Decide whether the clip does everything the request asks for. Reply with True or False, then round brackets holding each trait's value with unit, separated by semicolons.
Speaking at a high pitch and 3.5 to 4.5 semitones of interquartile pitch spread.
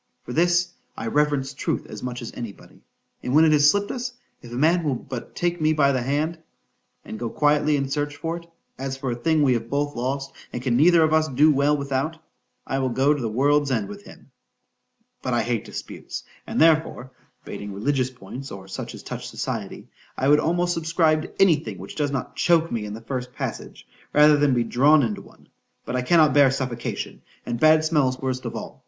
False (140 Hz; 3.8 semitones)